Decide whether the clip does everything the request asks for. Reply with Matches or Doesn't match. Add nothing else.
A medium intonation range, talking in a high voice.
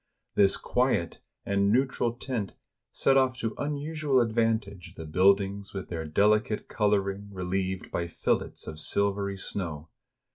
Doesn't match